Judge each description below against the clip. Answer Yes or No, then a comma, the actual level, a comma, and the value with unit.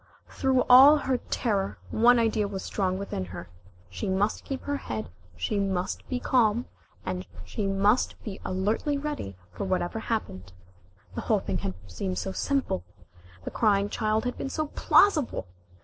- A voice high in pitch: Yes, high, 210 Hz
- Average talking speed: Yes, average, 155 wpm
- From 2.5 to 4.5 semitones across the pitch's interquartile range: No, average, 5.1 semitones